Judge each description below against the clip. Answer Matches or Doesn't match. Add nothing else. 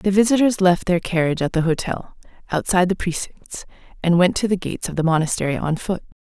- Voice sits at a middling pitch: Matches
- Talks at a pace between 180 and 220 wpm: Matches